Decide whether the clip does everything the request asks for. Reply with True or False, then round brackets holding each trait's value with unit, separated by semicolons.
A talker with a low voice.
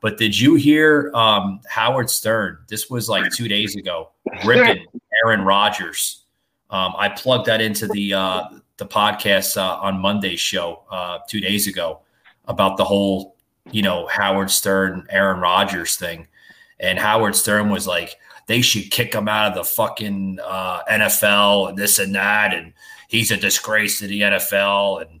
True (105 Hz)